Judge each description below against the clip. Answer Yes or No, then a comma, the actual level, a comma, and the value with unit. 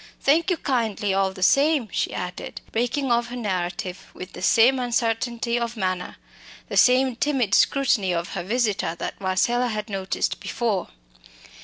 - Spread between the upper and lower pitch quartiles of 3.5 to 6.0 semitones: Yes, average, 4.6 semitones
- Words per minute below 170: Yes, average, 155 wpm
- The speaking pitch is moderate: No, high, 230 Hz